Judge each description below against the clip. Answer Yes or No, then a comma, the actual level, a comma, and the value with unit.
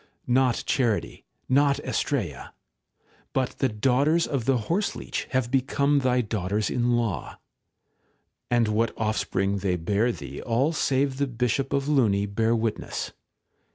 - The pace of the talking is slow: Yes, slow, 130 wpm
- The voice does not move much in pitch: No, average, 4.0 semitones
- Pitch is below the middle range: Yes, low, 120 Hz